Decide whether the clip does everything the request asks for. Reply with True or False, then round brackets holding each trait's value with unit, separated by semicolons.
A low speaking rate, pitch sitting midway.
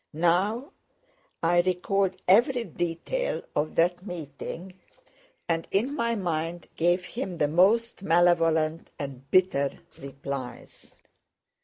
True (105 wpm; 175 Hz)